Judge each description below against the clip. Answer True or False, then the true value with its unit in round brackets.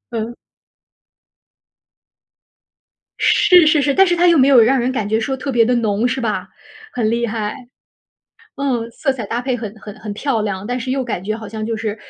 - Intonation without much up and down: False (3.5 semitones)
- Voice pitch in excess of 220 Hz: True (235 Hz)